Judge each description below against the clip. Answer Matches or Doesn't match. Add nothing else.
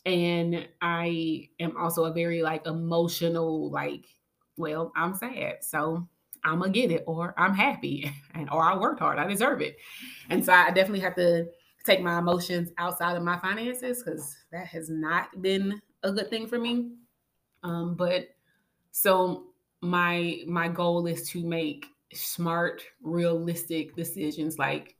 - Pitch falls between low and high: Matches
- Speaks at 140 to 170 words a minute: Matches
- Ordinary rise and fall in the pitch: Doesn't match